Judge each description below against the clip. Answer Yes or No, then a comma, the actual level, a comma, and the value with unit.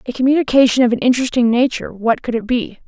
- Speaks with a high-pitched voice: Yes, high, 235 Hz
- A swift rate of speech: Yes, fast, 210 wpm